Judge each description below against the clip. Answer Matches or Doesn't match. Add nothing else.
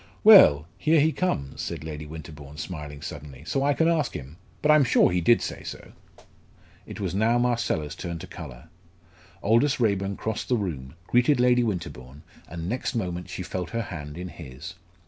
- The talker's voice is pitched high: Doesn't match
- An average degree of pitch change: Doesn't match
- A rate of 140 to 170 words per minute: Doesn't match